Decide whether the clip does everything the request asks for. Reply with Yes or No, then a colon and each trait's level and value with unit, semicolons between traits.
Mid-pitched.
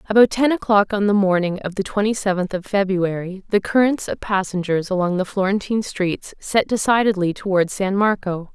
No: high, 195 Hz